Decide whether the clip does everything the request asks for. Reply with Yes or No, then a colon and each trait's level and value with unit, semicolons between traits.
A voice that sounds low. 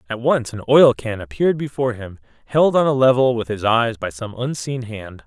Yes: low, 120 Hz